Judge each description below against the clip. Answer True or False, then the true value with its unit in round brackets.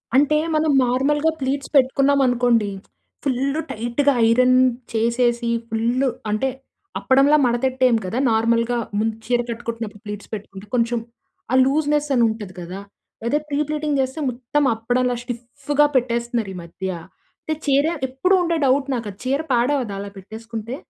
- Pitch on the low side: False (245 Hz)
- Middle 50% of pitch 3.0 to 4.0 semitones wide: True (3.3 semitones)